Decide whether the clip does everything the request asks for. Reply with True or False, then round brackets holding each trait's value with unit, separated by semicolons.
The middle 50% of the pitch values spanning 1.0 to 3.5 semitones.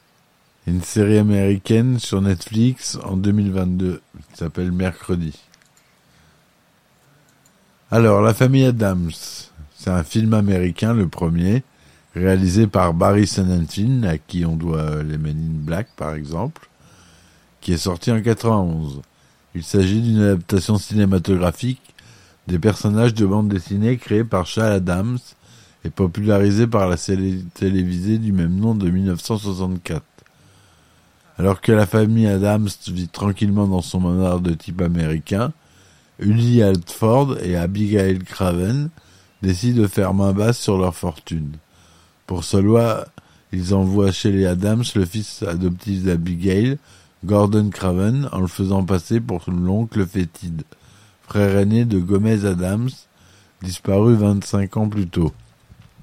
True (3.1 semitones)